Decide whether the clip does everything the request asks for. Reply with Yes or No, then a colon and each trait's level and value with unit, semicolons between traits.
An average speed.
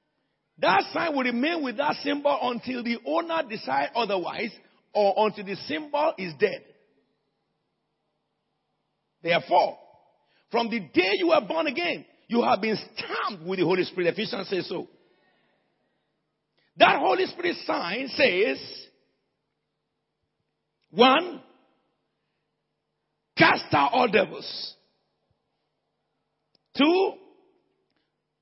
No: slow, 100 wpm